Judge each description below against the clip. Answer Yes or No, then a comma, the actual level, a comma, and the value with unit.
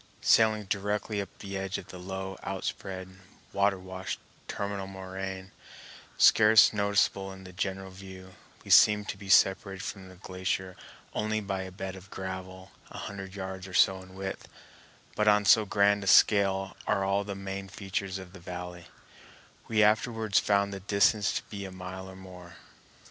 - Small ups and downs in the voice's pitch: Yes, narrow, 1.2 semitones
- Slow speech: No, average, 170 wpm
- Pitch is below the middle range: Yes, very low, 95 Hz